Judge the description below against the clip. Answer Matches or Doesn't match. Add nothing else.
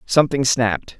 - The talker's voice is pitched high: Doesn't match